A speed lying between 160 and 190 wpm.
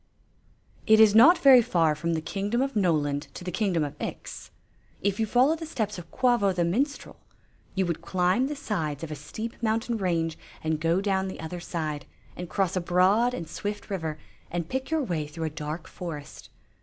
No: average, 200 wpm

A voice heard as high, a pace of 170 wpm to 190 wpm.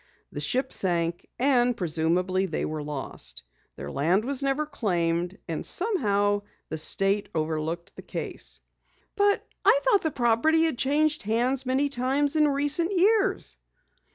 No: high, 235 Hz; average, 140 wpm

